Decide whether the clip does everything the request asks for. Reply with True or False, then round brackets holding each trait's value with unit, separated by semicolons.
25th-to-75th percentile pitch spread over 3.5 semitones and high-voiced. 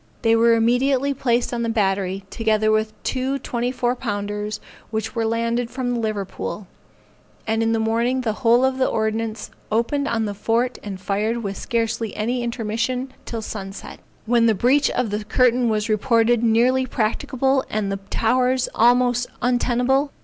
False (2.4 semitones; 230 Hz)